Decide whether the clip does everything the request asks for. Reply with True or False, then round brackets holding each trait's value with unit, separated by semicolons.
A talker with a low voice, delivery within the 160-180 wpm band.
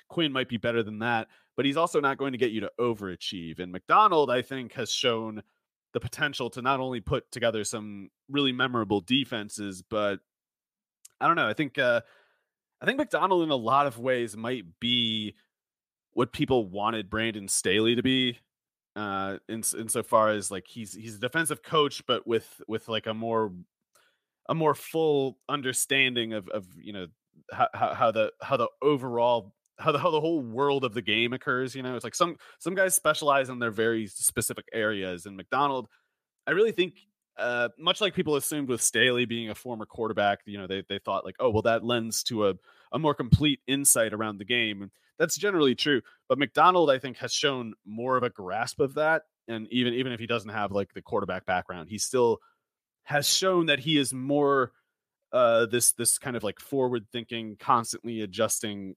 False (120 Hz; 195 wpm)